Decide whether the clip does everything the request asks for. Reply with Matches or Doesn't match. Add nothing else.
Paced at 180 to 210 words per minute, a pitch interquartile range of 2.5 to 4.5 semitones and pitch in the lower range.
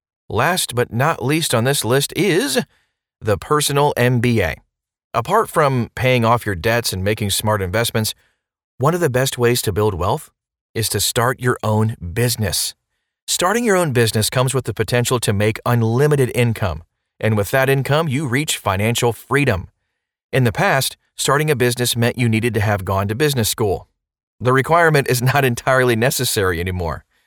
Doesn't match